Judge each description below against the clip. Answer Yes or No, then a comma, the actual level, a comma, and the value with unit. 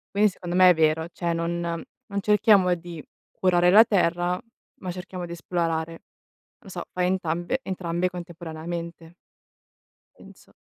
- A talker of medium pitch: Yes, medium, 175 Hz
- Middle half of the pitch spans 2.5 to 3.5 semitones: No, narrow, 1.7 semitones